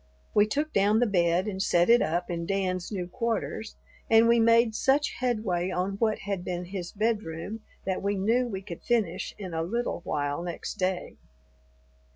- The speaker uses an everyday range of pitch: Yes, average, 4.2 semitones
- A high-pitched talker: Yes, high, 195 Hz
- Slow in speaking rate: No, average, 180 wpm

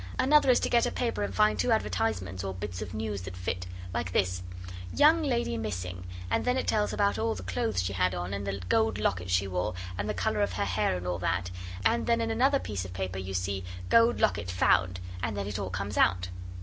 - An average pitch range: Yes, average, 3.3 semitones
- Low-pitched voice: Yes, low, 100 Hz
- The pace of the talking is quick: Yes, fast, 240 wpm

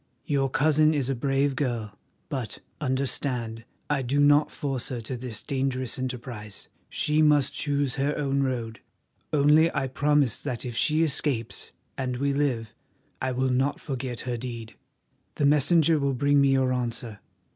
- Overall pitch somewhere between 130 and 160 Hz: Yes, low, 135 Hz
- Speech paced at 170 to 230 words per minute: No, average, 155 wpm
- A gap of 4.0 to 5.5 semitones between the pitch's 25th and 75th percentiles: No, average, 2.7 semitones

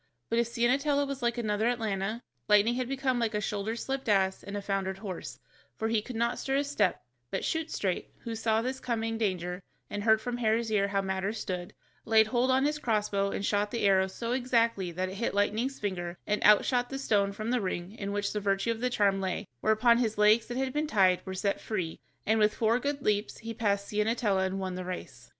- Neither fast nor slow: No, fast, 225 wpm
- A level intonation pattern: No, average, 3.3 semitones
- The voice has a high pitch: Yes, high, 215 Hz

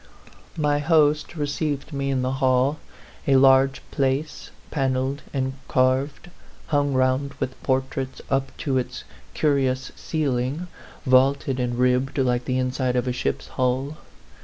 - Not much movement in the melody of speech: Yes, narrow, 1.8 semitones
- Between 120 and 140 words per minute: Yes, slow, 135 wpm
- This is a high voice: No, low, 135 Hz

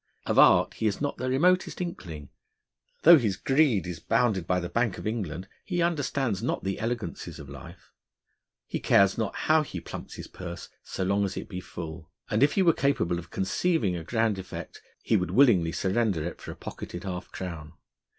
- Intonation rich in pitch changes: Yes, wide, 6.4 semitones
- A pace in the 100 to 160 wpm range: No, average, 195 wpm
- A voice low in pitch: Yes, low, 100 Hz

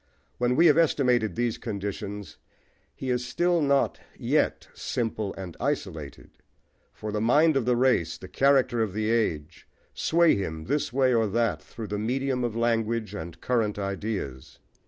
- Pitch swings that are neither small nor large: Yes, average, 4.1 semitones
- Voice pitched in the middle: No, low, 115 Hz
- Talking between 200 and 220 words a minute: No, average, 155 wpm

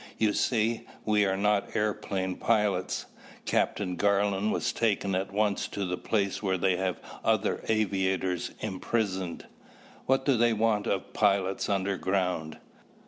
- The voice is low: Yes, low, 100 Hz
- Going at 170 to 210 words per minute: No, slow, 135 wpm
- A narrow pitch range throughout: Yes, narrow, 2.3 semitones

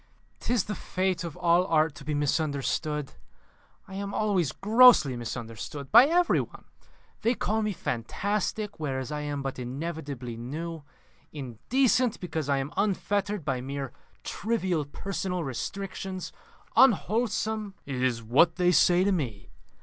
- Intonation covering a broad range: Yes, wide, 6.6 semitones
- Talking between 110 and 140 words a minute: Yes, slow, 135 wpm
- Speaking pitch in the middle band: Yes, medium, 170 Hz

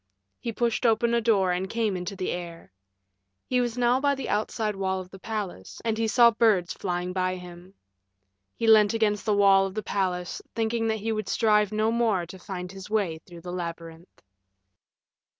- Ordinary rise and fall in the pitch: Yes, average, 3.6 semitones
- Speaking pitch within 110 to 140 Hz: No, high, 205 Hz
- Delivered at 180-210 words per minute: Yes, average, 190 wpm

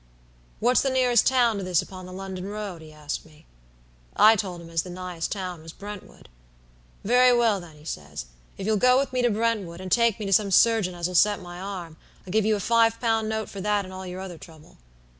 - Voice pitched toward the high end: Yes, high, 195 Hz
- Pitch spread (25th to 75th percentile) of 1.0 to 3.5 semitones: No, average, 4.0 semitones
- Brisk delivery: Yes, fast, 230 wpm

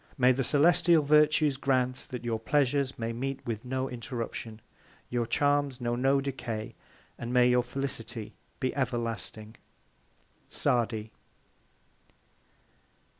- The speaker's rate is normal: No, slow, 115 wpm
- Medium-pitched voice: No, low, 125 Hz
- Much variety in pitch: No, average, 2.8 semitones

